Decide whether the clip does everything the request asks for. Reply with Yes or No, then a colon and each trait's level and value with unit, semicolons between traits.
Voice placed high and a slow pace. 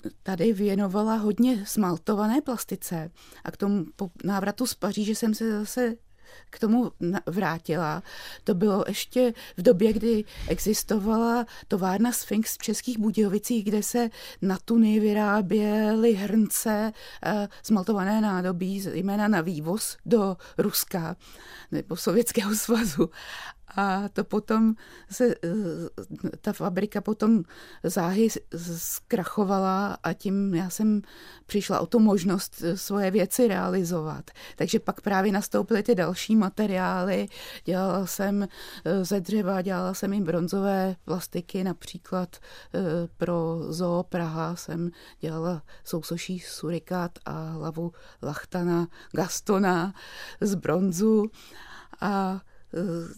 Yes: high, 195 Hz; slow, 110 wpm